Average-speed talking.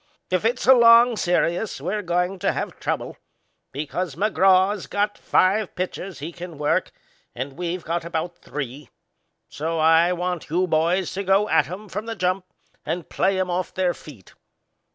Yes: average, 165 wpm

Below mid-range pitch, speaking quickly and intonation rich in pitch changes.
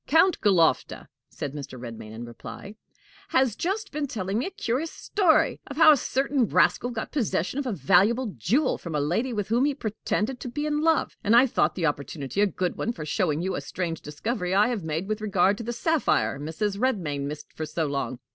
No: high, 210 Hz; fast, 215 wpm; wide, 8.5 semitones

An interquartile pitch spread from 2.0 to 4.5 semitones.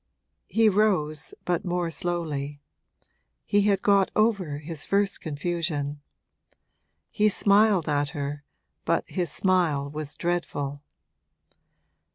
No: average, 5.2 semitones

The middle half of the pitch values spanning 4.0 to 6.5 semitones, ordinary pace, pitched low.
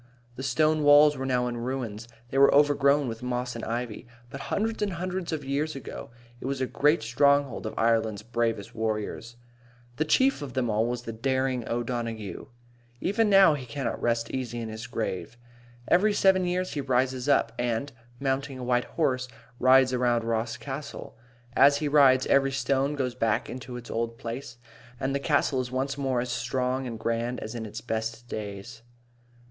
No: average, 3.2 semitones; average, 185 wpm; low, 125 Hz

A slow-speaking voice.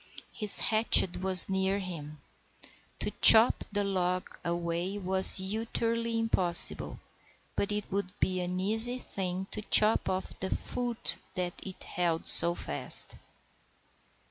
Yes: slow, 125 wpm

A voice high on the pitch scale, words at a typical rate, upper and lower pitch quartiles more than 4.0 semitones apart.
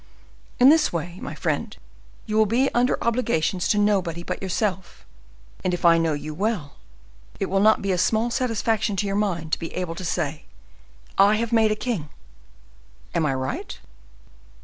Yes: high, 195 Hz; average, 175 wpm; average, 4.7 semitones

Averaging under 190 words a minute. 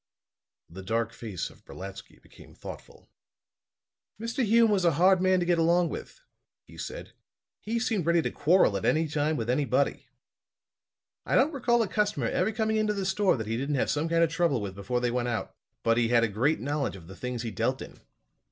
No: fast, 205 wpm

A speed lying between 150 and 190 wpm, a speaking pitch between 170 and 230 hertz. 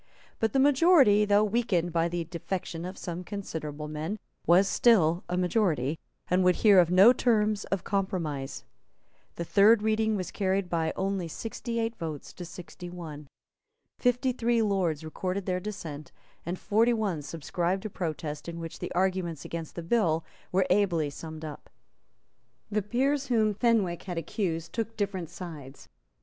Yes: average, 160 wpm; medium, 185 Hz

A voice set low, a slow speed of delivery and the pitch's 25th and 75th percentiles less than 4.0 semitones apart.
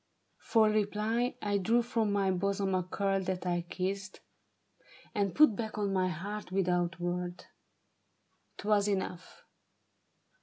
No: high, 195 Hz; slow, 125 wpm; narrow, 2.4 semitones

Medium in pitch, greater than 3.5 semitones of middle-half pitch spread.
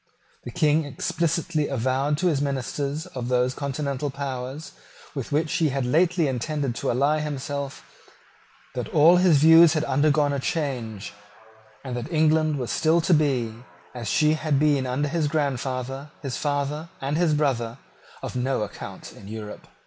No: medium, 145 Hz; average, 3.0 semitones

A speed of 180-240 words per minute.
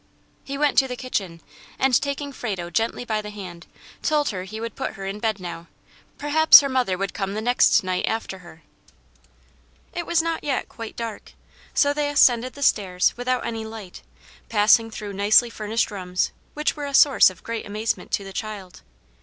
Yes: average, 185 wpm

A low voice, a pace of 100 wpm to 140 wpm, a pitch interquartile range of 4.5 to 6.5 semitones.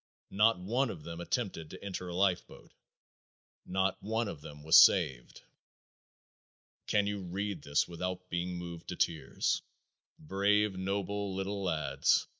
No: very low, 95 Hz; slow, 135 wpm; average, 2.9 semitones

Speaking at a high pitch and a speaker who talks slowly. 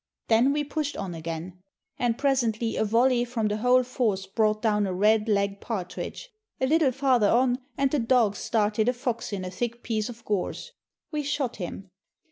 No: high, 230 Hz; average, 185 wpm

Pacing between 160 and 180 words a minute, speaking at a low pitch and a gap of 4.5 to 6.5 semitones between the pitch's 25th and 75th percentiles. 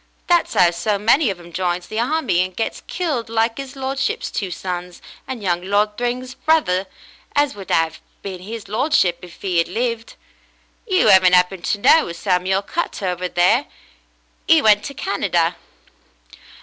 No: average, 165 wpm; high, 200 Hz; wide, 5.5 semitones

